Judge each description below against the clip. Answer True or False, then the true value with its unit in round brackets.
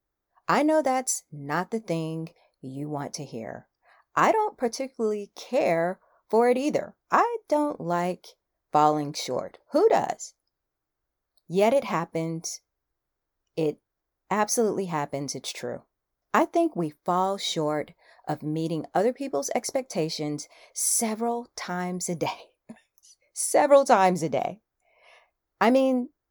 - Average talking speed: False (120 wpm)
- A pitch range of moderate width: False (7.6 semitones)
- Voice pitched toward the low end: False (180 Hz)